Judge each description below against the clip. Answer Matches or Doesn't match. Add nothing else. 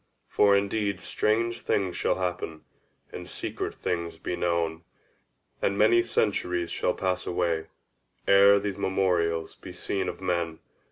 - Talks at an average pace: Doesn't match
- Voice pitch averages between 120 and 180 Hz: Doesn't match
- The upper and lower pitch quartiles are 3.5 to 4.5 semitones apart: Doesn't match